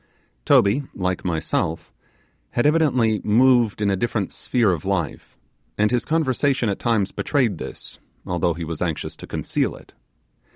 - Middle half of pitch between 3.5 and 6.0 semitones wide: Yes, average, 5.2 semitones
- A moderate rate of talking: Yes, average, 150 wpm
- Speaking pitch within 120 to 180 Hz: No, low, 105 Hz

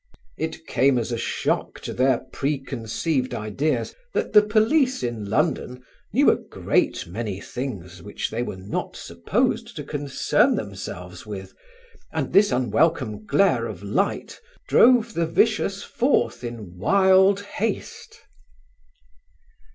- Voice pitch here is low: Yes, low, 130 Hz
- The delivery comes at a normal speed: No, slow, 125 wpm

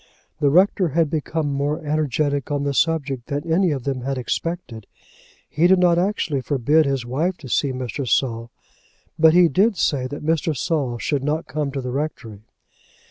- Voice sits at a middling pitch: Yes, medium, 145 Hz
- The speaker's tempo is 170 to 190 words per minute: Yes, average, 180 wpm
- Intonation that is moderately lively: Yes, average, 3.4 semitones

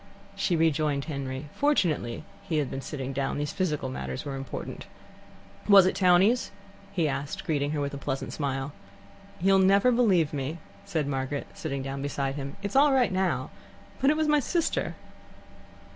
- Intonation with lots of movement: Yes, wide, 5.8 semitones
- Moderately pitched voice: Yes, medium, 150 Hz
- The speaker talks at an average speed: Yes, average, 165 wpm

